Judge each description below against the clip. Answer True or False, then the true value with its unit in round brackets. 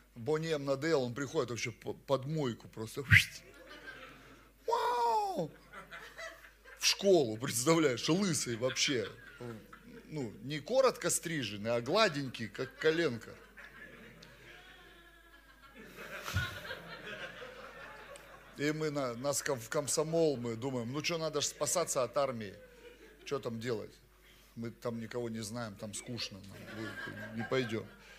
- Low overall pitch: False (145 Hz)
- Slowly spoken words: True (105 wpm)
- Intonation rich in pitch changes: True (6.3 semitones)